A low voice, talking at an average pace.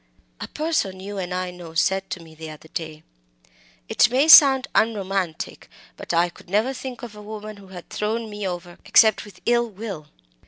No: high, 195 Hz; average, 190 wpm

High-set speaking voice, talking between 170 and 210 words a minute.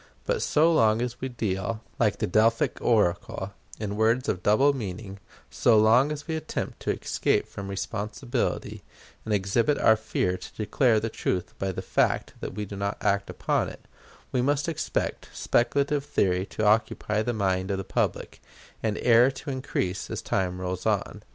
No: low, 110 Hz; average, 175 wpm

